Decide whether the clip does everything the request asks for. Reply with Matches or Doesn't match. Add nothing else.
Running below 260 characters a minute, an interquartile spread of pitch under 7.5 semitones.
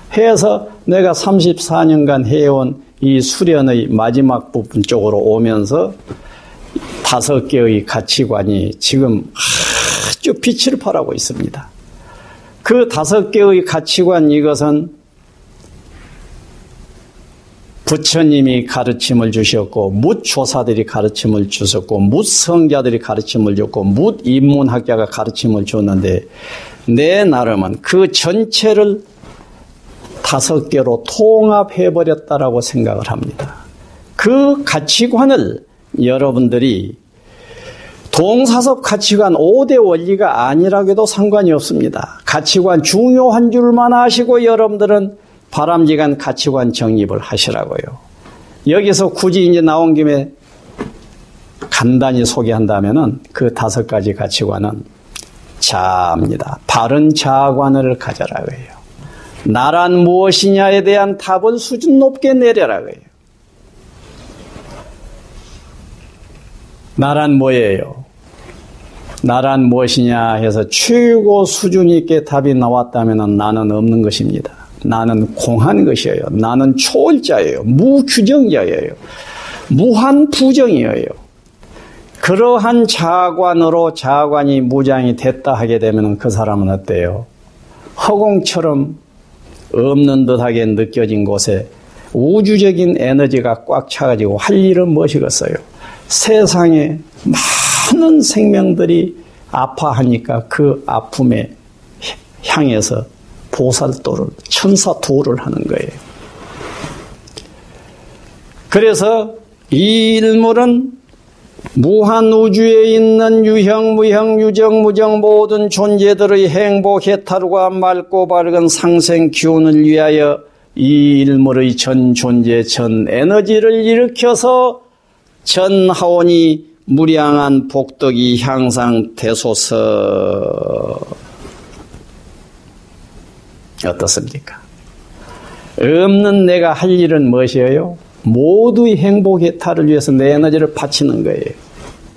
Doesn't match